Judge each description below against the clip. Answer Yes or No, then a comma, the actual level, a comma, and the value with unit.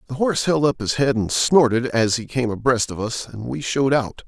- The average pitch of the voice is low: Yes, low, 125 Hz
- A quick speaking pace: Yes, fast, 255 wpm